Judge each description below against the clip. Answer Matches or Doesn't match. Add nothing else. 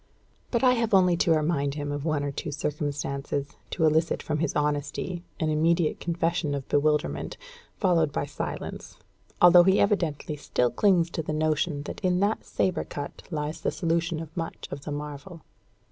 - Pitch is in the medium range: Matches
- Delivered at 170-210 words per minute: Matches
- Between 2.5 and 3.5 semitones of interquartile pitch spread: Matches